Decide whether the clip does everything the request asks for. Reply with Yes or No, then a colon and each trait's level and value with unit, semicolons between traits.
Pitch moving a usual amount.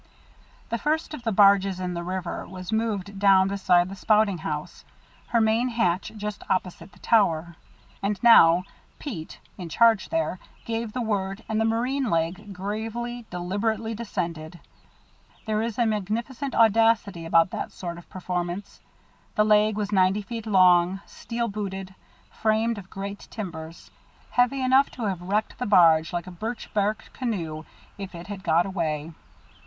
Yes: average, 3.9 semitones